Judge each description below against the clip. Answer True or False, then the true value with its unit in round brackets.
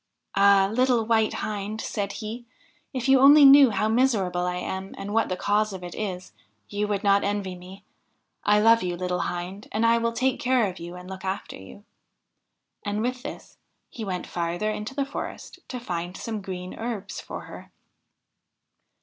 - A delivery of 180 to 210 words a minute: True (185 wpm)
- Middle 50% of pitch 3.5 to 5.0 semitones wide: True (3.8 semitones)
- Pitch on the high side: True (205 Hz)